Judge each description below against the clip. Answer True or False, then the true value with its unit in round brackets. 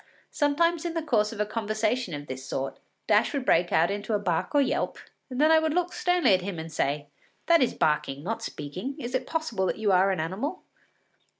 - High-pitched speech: True (215 Hz)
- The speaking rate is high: True (225 wpm)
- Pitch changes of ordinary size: False (8.8 semitones)